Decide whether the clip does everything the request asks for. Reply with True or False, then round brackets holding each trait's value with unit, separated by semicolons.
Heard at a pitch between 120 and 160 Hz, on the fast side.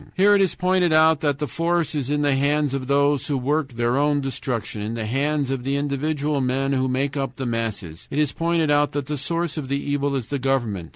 True (140 Hz; 240 wpm)